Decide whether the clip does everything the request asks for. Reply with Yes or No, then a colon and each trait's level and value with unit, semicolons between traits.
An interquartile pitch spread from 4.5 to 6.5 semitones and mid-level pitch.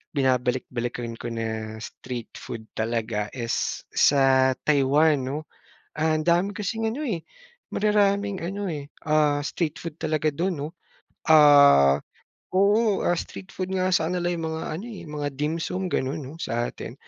Yes: wide, 5.6 semitones; medium, 150 Hz